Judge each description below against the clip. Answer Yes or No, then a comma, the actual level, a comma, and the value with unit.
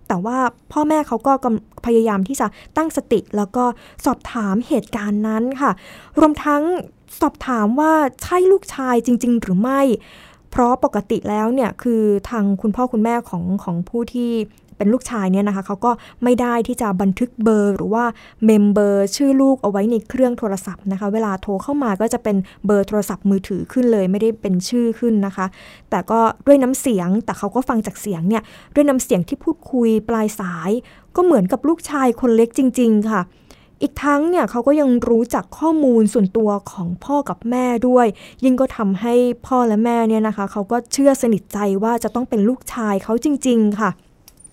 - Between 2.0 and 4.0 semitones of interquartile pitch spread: Yes, average, 3.5 semitones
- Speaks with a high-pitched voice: Yes, high, 230 Hz